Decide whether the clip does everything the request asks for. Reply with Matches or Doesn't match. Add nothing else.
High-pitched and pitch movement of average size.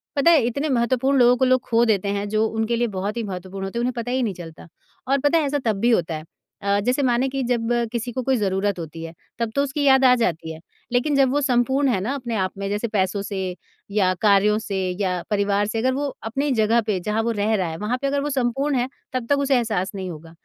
Matches